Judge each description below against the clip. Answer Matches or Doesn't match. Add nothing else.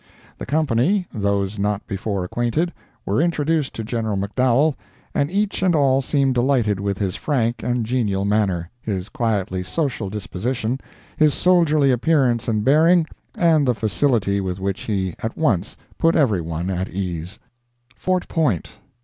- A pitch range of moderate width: Doesn't match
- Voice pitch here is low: Matches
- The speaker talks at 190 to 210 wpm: Doesn't match